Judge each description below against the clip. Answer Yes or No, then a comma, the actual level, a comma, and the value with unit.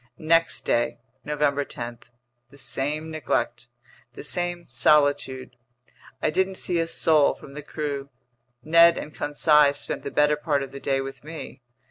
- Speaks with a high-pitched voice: No, medium, 150 Hz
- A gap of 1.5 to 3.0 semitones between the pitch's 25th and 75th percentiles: Yes, narrow, 2.4 semitones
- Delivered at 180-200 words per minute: No, average, 150 wpm